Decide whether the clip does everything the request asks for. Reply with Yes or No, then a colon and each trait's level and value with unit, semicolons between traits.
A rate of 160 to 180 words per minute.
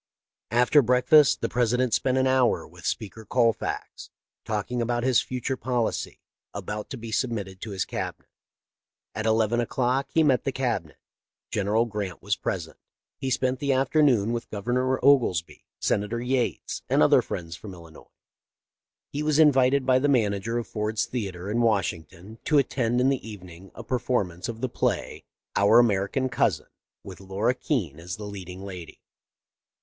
Yes: average, 165 wpm